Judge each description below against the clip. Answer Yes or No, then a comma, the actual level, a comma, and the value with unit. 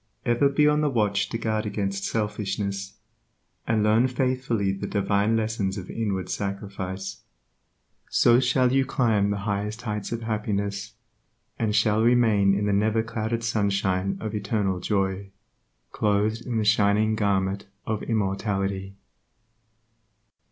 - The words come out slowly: Yes, slow, 130 wpm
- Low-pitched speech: Yes, low, 105 Hz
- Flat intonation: Yes, narrow, 2.2 semitones